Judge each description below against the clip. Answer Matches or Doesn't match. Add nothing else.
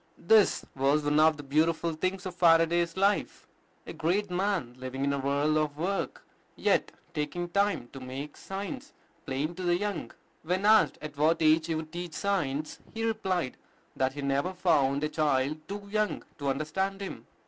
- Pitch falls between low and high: Matches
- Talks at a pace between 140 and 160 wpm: Doesn't match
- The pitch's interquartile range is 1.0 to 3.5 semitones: Doesn't match